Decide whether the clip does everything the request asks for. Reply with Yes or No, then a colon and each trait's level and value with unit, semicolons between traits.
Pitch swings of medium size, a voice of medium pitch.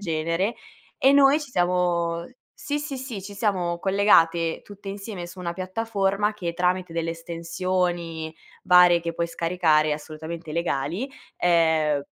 Yes: average, 3.0 semitones; medium, 175 Hz